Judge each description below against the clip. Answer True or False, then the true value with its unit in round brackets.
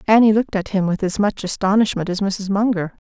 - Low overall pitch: False (200 Hz)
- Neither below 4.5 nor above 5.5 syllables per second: False (6.0 syllables/s)